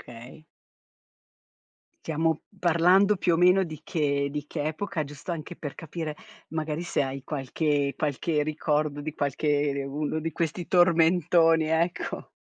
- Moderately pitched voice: Yes, medium, 155 Hz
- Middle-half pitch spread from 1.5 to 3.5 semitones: Yes, narrow, 2.4 semitones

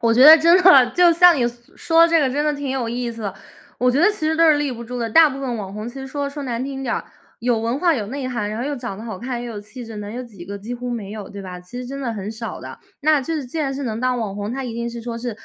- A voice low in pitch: No, high, 245 Hz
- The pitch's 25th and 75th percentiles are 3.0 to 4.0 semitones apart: Yes, average, 3.6 semitones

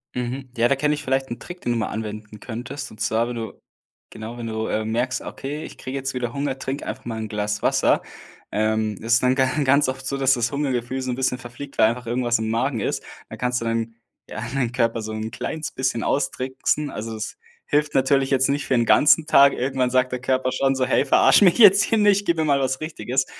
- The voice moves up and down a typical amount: Yes, average, 3.0 semitones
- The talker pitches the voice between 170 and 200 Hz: No, low, 130 Hz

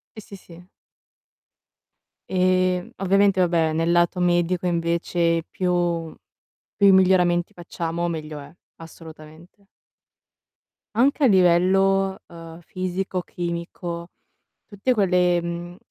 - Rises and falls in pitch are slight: Yes, narrow, 1.8 semitones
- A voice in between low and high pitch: Yes, medium, 175 Hz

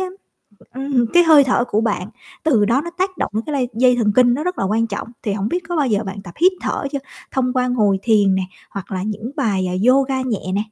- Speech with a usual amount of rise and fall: Yes, average, 5.0 semitones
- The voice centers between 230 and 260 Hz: Yes, high, 240 Hz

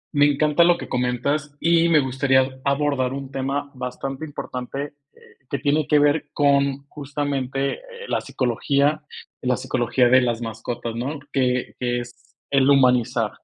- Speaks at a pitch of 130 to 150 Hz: Yes, low, 135 Hz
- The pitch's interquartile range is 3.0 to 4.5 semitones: No, narrow, 2.4 semitones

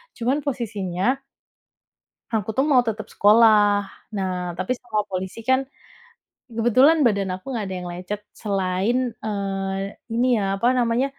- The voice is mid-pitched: No, high, 210 Hz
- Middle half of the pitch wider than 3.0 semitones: Yes, average, 3.8 semitones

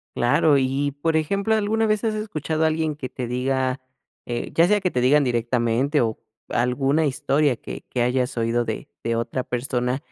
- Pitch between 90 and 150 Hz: Yes, low, 135 Hz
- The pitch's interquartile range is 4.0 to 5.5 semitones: Yes, average, 4.3 semitones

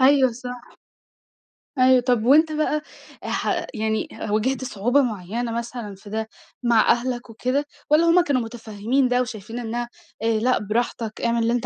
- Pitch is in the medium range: No, high, 240 Hz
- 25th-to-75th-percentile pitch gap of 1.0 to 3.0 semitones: Yes, narrow, 2.6 semitones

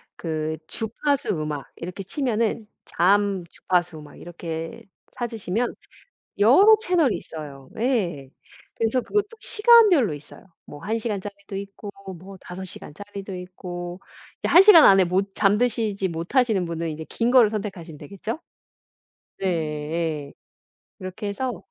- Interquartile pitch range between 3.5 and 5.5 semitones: Yes, average, 5.2 semitones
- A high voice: Yes, high, 195 Hz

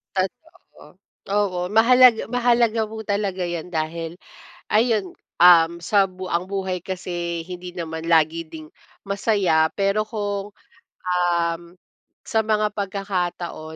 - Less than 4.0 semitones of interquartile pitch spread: Yes, average, 3.6 semitones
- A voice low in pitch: No, medium, 185 Hz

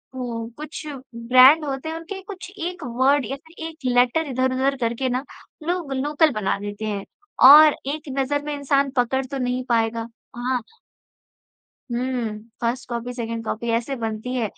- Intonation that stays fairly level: No, average, 3.5 semitones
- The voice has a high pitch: Yes, very high, 255 Hz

